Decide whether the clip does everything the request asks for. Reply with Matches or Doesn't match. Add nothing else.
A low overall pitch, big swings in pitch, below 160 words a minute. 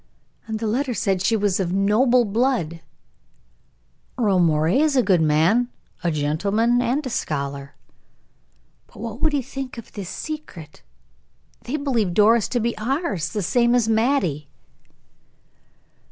Doesn't match